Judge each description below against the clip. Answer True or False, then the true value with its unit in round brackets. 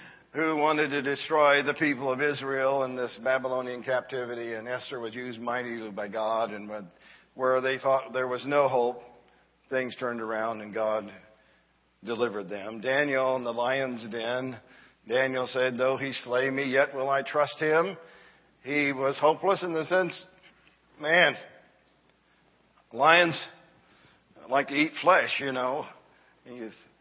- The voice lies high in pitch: False (130 Hz)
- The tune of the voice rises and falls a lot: False (2.9 semitones)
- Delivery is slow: False (145 wpm)